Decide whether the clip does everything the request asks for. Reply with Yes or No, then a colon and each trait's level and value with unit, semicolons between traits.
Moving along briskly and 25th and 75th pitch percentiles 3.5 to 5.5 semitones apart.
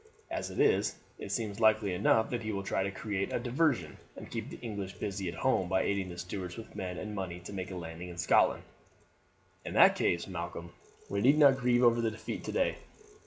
Yes: fast, 215 wpm; average, 3.9 semitones